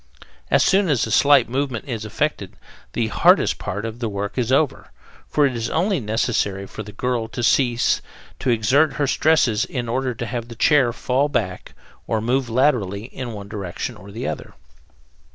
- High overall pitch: No, low, 120 Hz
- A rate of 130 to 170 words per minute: No, average, 185 wpm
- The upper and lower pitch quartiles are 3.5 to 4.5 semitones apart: Yes, average, 3.8 semitones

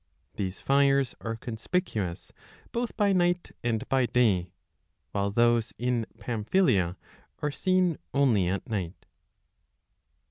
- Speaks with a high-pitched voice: No, low, 120 Hz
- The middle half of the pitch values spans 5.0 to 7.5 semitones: Yes, wide, 5.6 semitones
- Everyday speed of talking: No, slow, 115 wpm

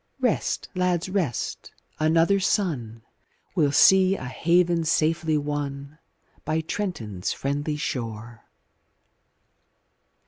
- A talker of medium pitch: Yes, medium, 155 Hz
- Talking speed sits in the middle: No, slow, 90 wpm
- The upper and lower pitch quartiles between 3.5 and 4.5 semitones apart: Yes, average, 4.2 semitones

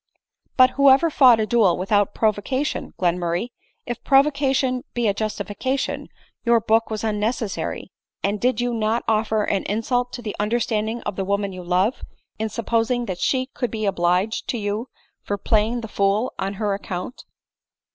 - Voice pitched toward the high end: Yes, high, 220 Hz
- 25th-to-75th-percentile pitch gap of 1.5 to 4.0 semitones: Yes, average, 3.2 semitones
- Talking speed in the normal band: Yes, average, 160 wpm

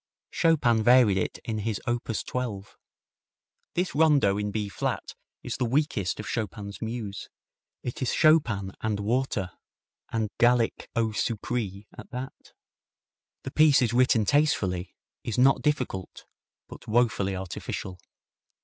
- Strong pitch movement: No, average, 4.0 semitones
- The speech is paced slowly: Yes, slow, 130 wpm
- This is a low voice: Yes, low, 115 Hz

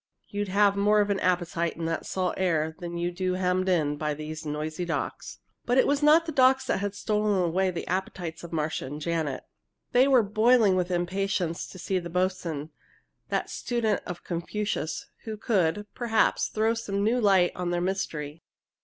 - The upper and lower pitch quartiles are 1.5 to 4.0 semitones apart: Yes, average, 3.7 semitones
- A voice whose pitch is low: No, medium, 185 Hz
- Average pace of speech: Yes, average, 185 wpm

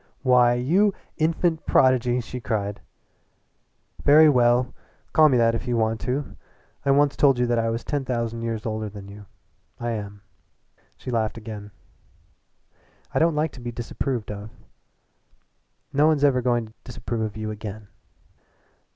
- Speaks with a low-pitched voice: Yes, low, 120 Hz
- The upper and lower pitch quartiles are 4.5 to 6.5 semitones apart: No, average, 3.6 semitones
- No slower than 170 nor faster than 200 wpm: No, average, 155 wpm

